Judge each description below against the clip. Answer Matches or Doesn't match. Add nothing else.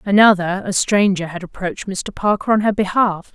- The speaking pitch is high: Matches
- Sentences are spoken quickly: Doesn't match